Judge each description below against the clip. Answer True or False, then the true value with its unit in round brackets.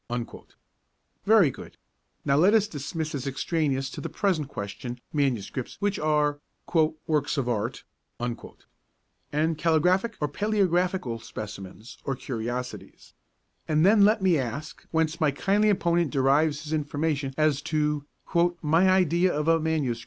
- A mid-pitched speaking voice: True (155 Hz)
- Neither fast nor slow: False (130 wpm)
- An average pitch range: True (4.2 semitones)